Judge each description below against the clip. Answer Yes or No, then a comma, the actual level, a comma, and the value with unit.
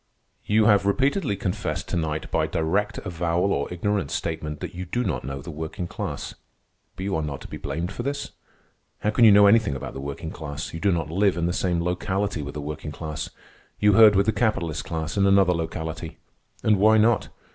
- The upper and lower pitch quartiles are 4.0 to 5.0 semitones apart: Yes, average, 4.4 semitones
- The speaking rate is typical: No, fast, 210 wpm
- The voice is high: No, very low, 90 Hz